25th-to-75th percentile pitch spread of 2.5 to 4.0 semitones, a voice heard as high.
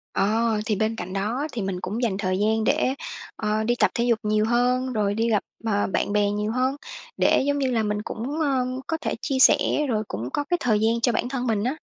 Yes: average, 3.3 semitones; high, 225 Hz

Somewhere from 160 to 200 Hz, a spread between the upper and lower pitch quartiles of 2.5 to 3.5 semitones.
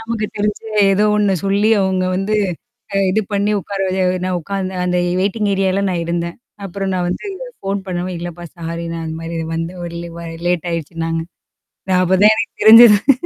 Yes: medium, 185 Hz; average, 2.9 semitones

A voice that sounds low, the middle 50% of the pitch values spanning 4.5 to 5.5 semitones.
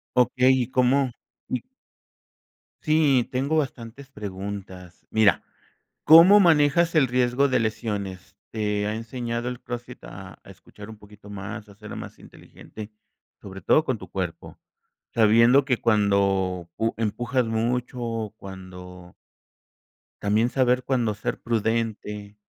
No: low, 115 Hz; average, 3.8 semitones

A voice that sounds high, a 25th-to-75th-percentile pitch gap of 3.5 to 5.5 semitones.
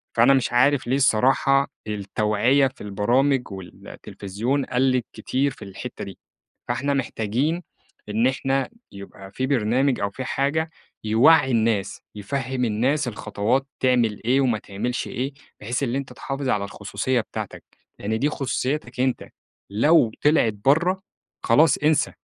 No: low, 125 Hz; average, 4.2 semitones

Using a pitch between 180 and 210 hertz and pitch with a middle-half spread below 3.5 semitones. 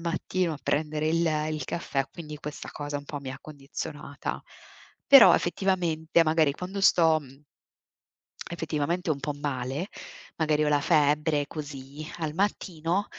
No: medium, 155 Hz; average, 2.7 semitones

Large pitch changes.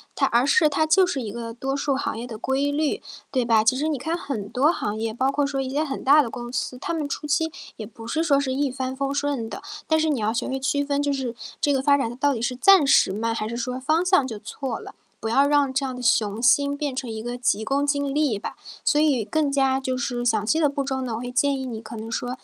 No: average, 3.3 semitones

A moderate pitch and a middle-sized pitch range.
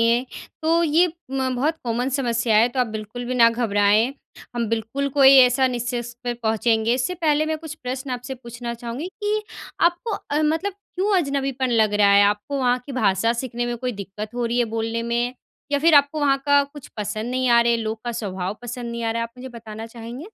No: high, 245 Hz; average, 3.3 semitones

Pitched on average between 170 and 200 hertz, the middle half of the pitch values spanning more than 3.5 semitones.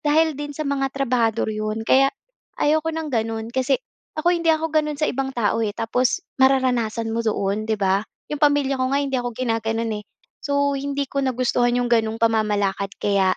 No: very high, 250 Hz; average, 4.1 semitones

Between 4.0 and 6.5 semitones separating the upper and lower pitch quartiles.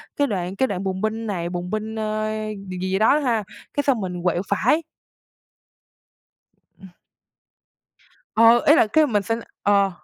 No: average, 3.3 semitones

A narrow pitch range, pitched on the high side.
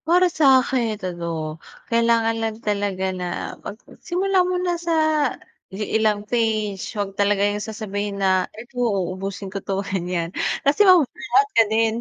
No: average, 4.0 semitones; high, 210 Hz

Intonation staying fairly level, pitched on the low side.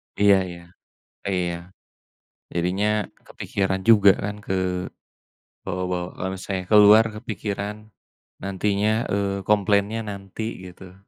Yes: narrow, 1.8 semitones; low, 100 Hz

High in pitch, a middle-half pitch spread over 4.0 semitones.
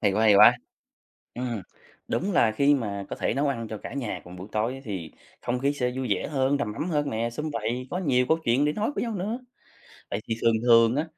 No: low, 125 Hz; average, 4.6 semitones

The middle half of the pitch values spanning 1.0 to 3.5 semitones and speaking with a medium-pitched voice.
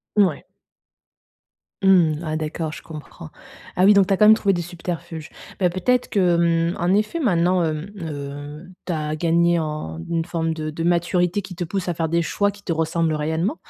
Yes: average, 2.8 semitones; medium, 170 Hz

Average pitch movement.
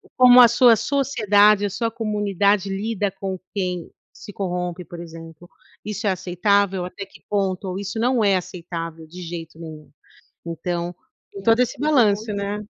Yes: average, 3.1 semitones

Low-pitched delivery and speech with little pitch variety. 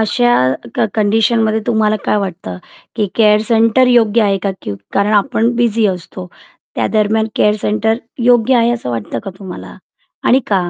No: high, 215 Hz; narrow, 2.3 semitones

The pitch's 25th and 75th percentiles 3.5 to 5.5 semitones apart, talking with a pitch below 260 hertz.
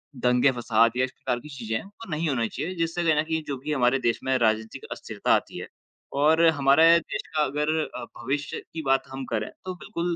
Yes: average, 4.6 semitones; low, 135 Hz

